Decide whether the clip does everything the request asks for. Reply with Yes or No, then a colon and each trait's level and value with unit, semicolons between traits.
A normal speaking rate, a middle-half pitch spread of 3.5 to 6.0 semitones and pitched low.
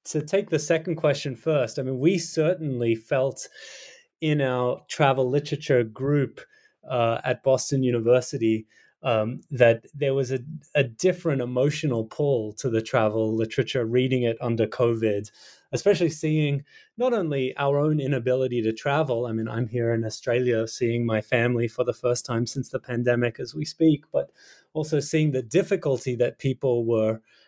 Yes: average, 160 wpm; average, 3.9 semitones; low, 130 Hz